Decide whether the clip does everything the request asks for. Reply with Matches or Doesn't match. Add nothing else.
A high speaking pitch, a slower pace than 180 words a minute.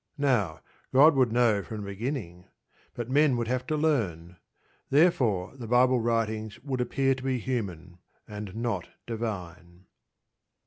Doesn't match